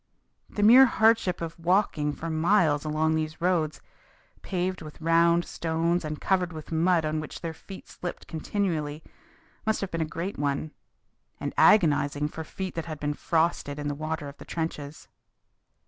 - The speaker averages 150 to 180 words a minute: Yes, average, 165 wpm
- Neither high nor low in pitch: Yes, medium, 160 Hz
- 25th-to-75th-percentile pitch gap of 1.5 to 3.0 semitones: Yes, narrow, 2.6 semitones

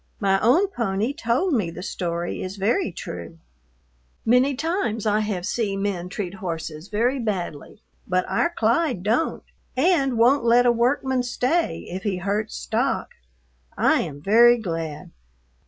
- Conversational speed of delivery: Yes, average, 145 wpm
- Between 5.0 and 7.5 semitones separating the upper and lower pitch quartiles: Yes, wide, 5.4 semitones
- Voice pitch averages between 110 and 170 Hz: No, high, 220 Hz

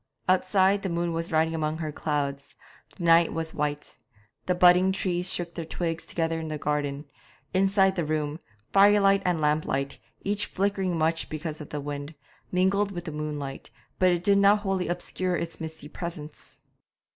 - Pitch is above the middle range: No, medium, 170 Hz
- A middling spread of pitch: Yes, average, 3.4 semitones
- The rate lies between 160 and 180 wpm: Yes, average, 165 wpm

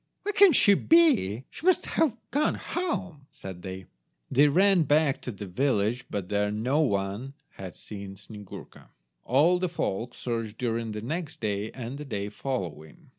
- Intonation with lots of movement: Yes, wide, 7.8 semitones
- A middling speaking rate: Yes, average, 165 wpm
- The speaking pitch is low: Yes, low, 120 Hz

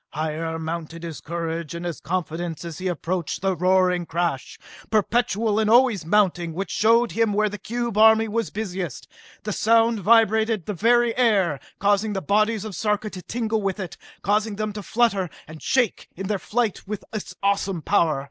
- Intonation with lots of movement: No, average, 4.3 semitones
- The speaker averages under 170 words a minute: No, average, 175 wpm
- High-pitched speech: Yes, high, 200 Hz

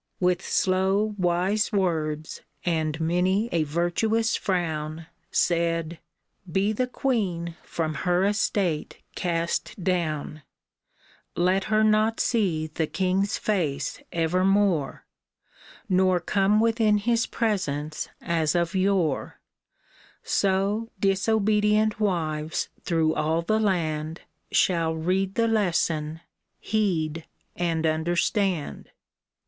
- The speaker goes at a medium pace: No, slow, 100 wpm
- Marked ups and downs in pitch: No, average, 4.1 semitones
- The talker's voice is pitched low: No, medium, 180 Hz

